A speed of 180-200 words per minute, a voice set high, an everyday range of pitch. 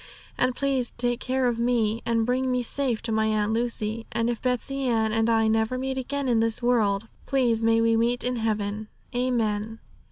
No: average, 195 wpm; high, 230 Hz; narrow, 2.1 semitones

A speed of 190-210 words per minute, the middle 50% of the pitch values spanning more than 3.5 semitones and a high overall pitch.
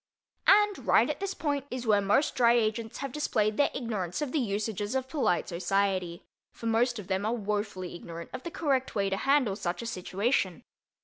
Yes: average, 195 wpm; average, 5.1 semitones; high, 220 Hz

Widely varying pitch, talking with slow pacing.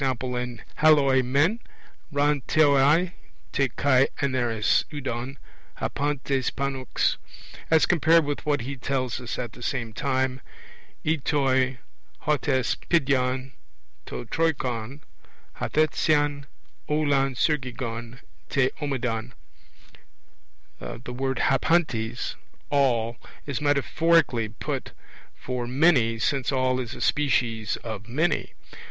No: average, 2.8 semitones; slow, 105 wpm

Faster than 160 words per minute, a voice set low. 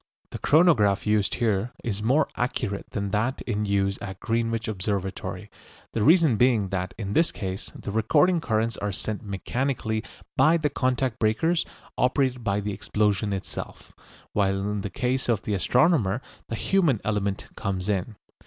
No: average, 155 wpm; low, 110 Hz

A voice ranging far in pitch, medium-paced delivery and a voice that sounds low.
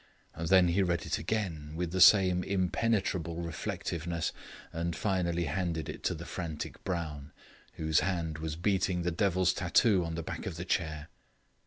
No: narrow, 2.4 semitones; average, 160 wpm; very low, 85 Hz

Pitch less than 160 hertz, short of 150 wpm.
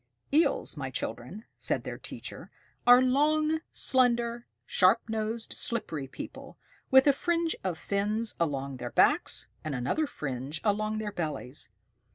No: high, 215 Hz; slow, 135 wpm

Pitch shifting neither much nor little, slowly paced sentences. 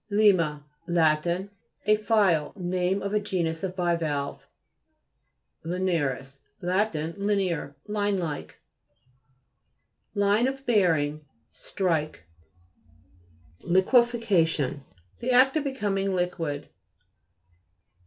Yes: average, 4.2 semitones; slow, 90 wpm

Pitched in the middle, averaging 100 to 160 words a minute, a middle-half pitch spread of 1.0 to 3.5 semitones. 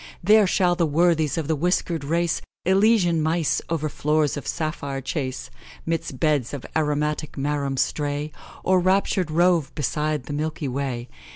Yes: medium, 155 Hz; average, 150 wpm; average, 2.9 semitones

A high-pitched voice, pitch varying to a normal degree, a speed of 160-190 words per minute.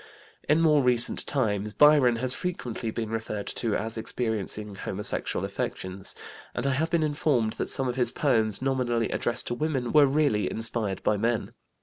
No: low, 120 Hz; average, 4.0 semitones; average, 165 wpm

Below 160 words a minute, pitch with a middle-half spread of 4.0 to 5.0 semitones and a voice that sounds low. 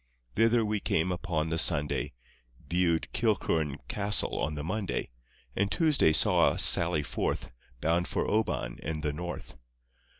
Yes: average, 140 wpm; average, 4.7 semitones; very low, 85 Hz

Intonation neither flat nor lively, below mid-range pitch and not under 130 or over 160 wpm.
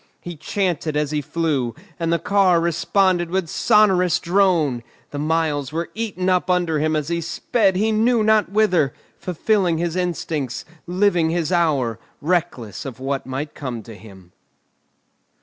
No: average, 4.0 semitones; medium, 170 Hz; average, 150 wpm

